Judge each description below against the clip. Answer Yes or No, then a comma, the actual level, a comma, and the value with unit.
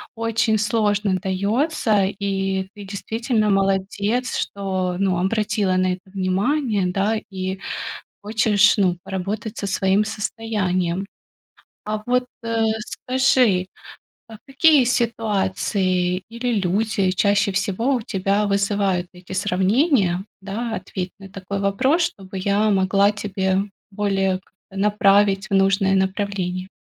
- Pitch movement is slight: Yes, narrow, 2.3 semitones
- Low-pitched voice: No, high, 200 Hz